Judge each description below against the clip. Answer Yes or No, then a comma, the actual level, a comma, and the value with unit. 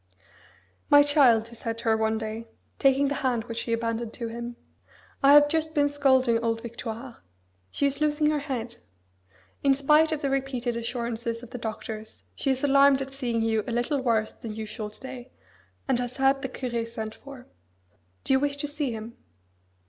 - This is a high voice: Yes, high, 245 Hz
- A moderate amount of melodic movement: Yes, average, 3.3 semitones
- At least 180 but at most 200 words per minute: Yes, average, 190 wpm